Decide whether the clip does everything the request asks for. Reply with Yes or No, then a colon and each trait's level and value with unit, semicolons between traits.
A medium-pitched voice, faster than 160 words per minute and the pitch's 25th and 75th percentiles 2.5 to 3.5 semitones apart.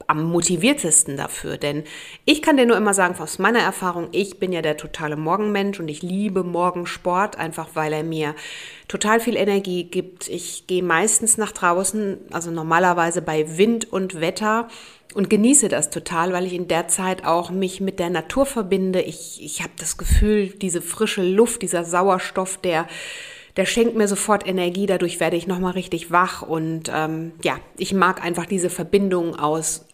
Yes: medium, 180 Hz; average, 175 wpm; average, 3.2 semitones